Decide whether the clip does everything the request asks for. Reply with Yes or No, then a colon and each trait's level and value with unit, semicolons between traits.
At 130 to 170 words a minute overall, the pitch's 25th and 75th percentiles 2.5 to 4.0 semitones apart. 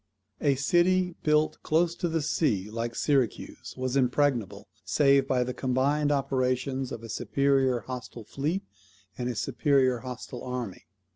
Yes: average, 140 wpm; average, 2.8 semitones